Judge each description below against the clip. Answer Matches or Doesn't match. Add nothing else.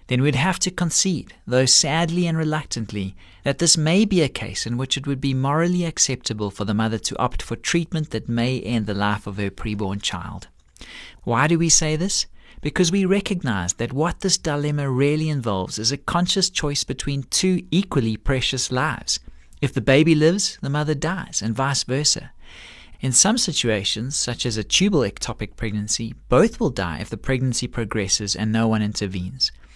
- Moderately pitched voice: Doesn't match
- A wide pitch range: Matches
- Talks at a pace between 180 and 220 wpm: Matches